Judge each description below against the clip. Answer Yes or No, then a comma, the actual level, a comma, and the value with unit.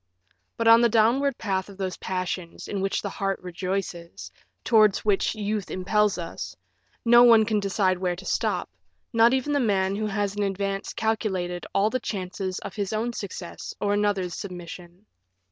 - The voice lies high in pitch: Yes, high, 200 Hz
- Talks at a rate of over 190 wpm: No, average, 170 wpm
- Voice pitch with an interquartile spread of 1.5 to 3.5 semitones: Yes, average, 2.7 semitones